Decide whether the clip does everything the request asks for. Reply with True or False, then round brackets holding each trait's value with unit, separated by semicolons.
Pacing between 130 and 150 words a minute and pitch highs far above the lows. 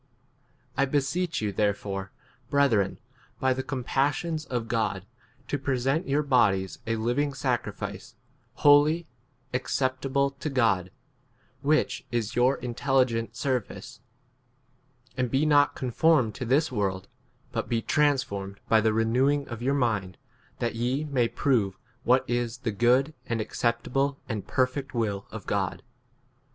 False (140 wpm; 3.7 semitones)